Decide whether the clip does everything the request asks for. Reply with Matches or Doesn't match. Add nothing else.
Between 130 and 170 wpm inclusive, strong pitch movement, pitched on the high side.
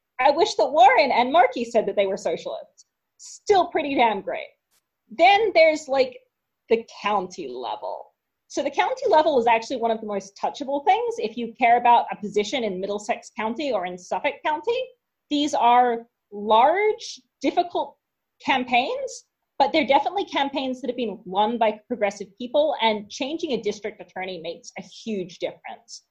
Matches